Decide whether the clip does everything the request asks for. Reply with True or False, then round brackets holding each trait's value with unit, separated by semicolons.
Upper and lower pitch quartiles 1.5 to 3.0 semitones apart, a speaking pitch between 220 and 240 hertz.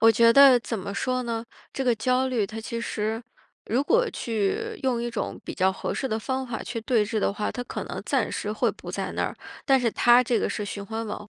True (2.7 semitones; 230 Hz)